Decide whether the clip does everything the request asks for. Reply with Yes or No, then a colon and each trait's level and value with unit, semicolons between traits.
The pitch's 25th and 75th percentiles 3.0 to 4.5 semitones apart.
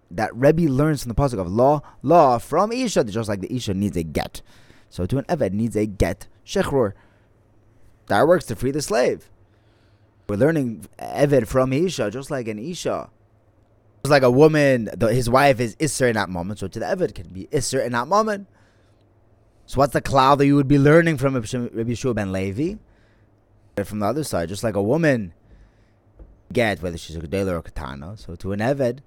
No: average, 5.1 semitones